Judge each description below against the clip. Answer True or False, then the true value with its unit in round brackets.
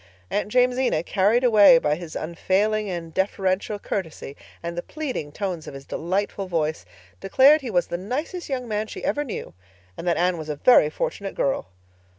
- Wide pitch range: True (6.0 semitones)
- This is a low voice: False (195 Hz)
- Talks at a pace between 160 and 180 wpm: True (175 wpm)